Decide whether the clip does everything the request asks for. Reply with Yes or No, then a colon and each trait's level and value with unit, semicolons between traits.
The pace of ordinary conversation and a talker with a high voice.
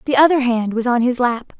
No: fast, 265 wpm; very high, 250 Hz